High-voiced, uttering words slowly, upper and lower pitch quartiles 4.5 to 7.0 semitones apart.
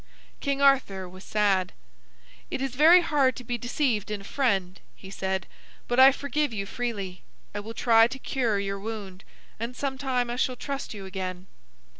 No: high, 230 Hz; average, 175 wpm; average, 5.2 semitones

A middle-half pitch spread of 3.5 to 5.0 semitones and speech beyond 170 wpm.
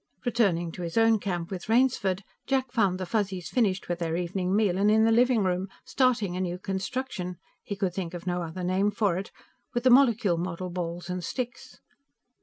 Yes: average, 4.0 semitones; average, 200 wpm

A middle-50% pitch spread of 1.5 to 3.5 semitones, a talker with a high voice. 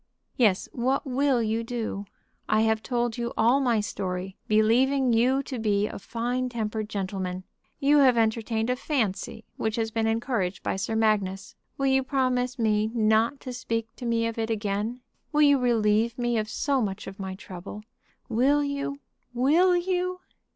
Yes: average, 3.2 semitones; high, 230 Hz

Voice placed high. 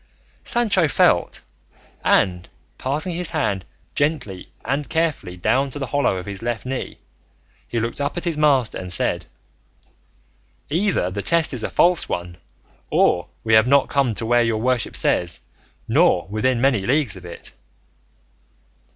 No: low, 125 Hz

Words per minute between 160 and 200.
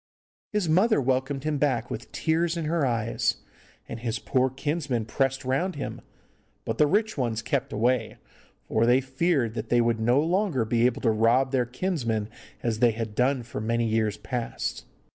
Yes: average, 180 wpm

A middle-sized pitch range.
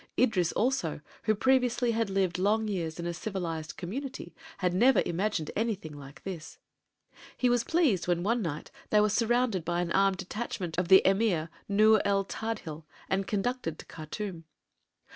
Yes: average, 4.6 semitones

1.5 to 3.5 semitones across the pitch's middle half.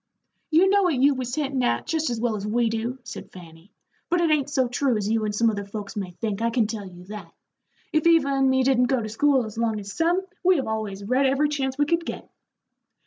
No: average, 5.0 semitones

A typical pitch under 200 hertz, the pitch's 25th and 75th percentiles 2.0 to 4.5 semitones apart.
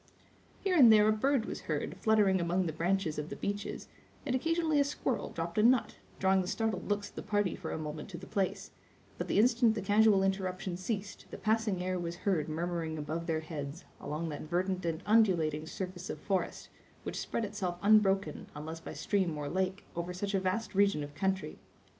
Yes: high, 190 Hz; average, 3.9 semitones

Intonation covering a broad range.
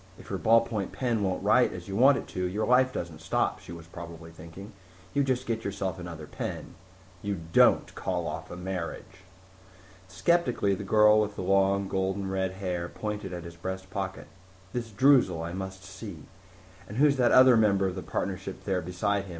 No: average, 2.9 semitones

